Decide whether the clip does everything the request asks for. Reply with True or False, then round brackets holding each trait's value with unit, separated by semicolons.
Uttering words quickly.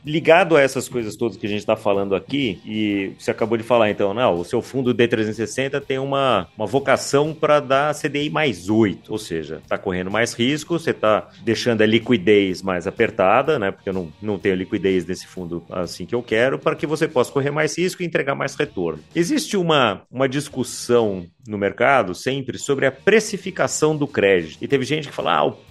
True (205 wpm)